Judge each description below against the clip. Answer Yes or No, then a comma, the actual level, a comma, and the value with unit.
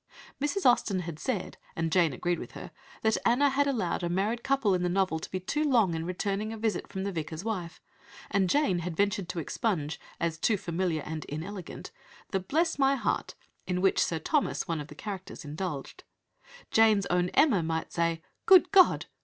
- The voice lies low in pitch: No, high, 190 Hz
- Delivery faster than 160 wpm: Yes, average, 195 wpm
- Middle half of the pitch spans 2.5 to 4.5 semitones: No, average, 4.9 semitones